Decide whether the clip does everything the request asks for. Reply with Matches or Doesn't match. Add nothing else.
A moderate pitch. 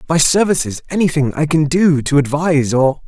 Matches